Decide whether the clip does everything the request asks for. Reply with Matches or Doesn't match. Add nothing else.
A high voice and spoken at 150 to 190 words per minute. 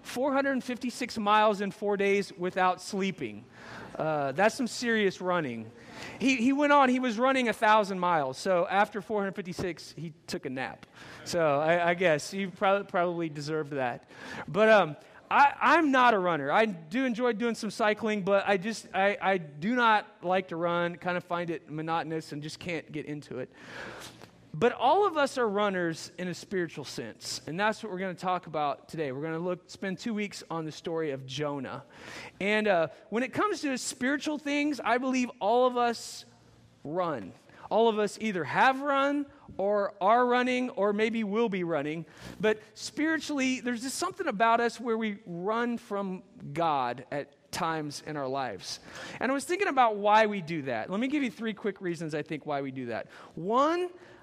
Doesn't match